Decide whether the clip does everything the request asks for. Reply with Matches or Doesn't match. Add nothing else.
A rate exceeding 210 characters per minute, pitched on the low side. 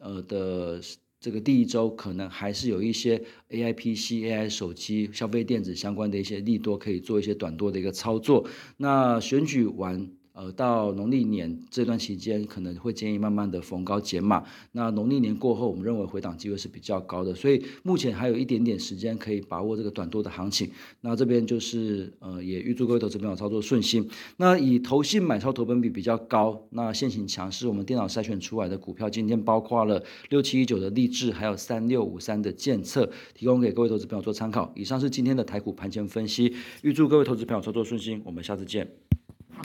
Matches